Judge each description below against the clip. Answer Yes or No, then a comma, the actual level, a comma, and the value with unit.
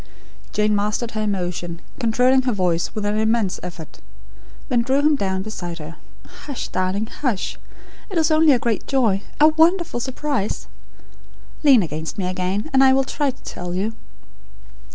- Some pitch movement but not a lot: No, wide, 6.2 semitones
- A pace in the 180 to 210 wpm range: No, average, 160 wpm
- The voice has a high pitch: Yes, high, 220 Hz